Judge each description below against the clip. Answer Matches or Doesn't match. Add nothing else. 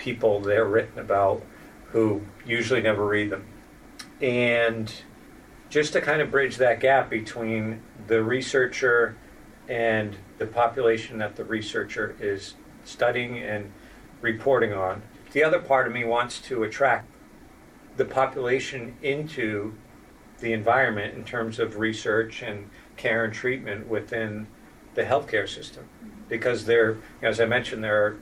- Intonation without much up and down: Matches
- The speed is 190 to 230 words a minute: Doesn't match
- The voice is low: Matches